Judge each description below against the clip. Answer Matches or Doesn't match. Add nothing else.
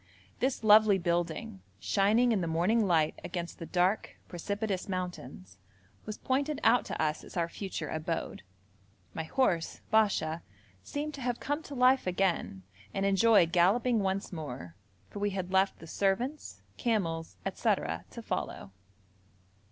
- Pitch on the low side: Doesn't match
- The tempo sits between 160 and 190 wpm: Doesn't match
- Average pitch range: Matches